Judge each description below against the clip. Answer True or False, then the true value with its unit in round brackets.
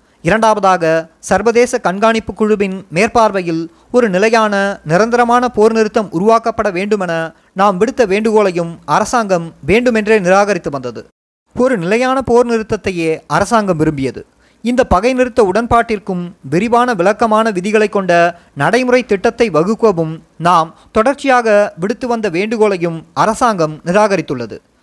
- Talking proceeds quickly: False (105 wpm)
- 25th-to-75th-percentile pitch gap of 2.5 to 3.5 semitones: False (4.8 semitones)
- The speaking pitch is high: True (215 Hz)